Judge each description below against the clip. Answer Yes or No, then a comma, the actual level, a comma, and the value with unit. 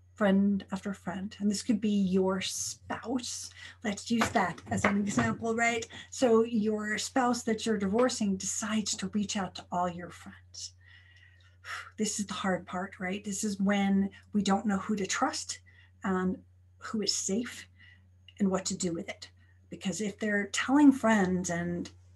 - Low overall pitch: No, high, 195 Hz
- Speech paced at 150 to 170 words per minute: Yes, average, 165 wpm